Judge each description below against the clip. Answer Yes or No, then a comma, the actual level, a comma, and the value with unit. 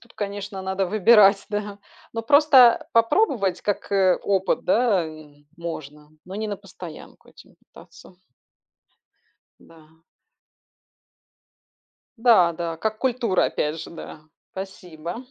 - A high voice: Yes, high, 195 Hz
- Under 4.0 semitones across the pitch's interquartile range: No, average, 4.4 semitones